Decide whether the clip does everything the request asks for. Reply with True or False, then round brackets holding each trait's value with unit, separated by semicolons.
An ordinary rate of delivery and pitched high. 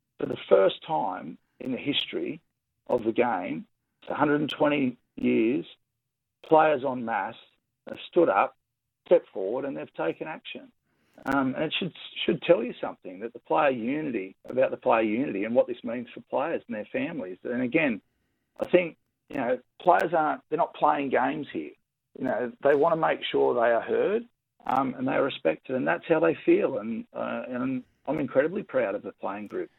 True (185 wpm; 235 Hz)